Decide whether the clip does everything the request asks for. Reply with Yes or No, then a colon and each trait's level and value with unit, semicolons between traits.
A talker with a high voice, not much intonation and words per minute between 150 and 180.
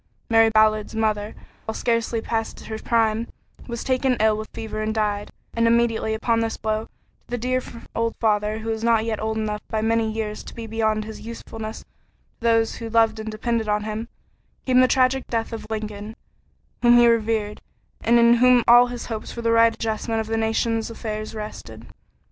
No: high, 225 Hz; narrow, 1.2 semitones; average, 190 wpm